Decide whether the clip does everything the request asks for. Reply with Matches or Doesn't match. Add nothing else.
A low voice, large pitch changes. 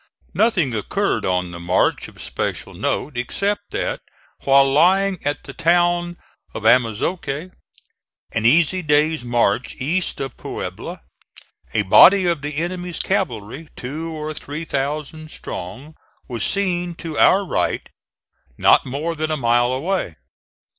Doesn't match